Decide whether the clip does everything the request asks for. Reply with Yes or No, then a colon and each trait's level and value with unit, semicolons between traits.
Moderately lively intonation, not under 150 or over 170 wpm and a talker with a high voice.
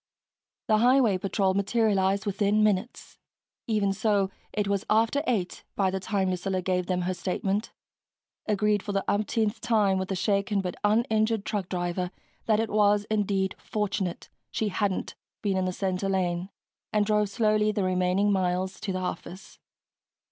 No: narrow, 2.2 semitones; average, 155 wpm; high, 200 Hz